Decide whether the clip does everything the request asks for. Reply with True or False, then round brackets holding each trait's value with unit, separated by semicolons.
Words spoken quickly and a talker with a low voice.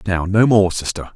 True (210 wpm; 100 Hz)